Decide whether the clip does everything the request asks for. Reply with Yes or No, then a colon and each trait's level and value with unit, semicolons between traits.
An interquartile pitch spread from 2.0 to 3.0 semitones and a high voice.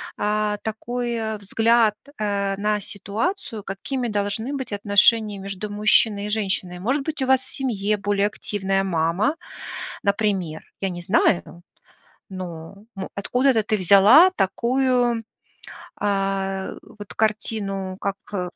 Yes: narrow, 2.6 semitones; high, 205 Hz